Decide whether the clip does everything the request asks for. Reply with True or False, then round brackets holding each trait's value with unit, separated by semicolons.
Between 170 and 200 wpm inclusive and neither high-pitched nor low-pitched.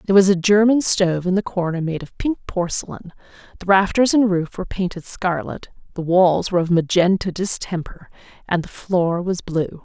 True (185 wpm; 180 Hz)